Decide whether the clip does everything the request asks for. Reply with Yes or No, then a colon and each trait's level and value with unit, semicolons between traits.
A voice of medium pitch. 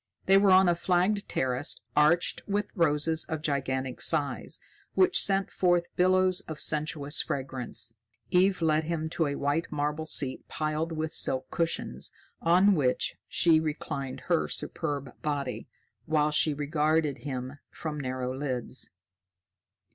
Yes: medium, 155 Hz